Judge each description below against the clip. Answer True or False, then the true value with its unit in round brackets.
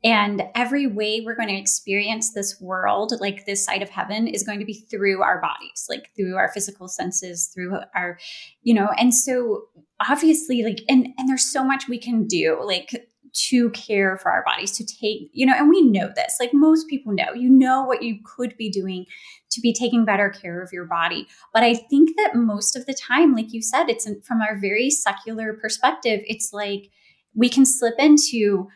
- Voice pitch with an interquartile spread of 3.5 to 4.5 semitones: True (4.1 semitones)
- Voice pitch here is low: False (225 Hz)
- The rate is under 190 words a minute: False (205 wpm)